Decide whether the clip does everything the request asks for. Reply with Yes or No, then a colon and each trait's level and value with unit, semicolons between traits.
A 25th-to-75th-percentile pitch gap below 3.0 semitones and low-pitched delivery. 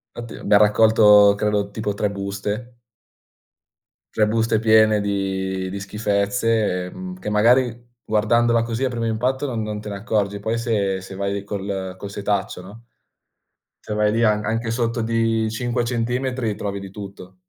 Yes: narrow, 2.4 semitones; low, 105 Hz